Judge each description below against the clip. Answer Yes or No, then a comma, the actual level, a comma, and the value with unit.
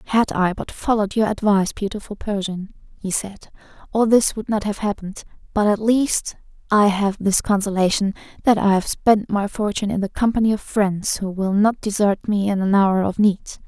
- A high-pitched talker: Yes, high, 205 Hz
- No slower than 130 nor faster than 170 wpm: No, average, 195 wpm